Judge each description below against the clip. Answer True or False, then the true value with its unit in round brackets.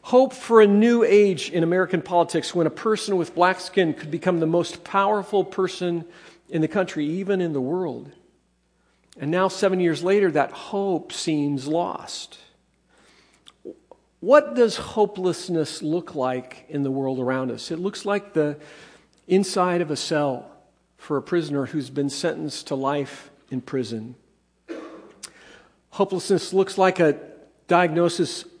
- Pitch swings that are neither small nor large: True (4.4 semitones)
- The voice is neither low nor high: True (175 Hz)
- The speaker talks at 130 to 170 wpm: True (145 wpm)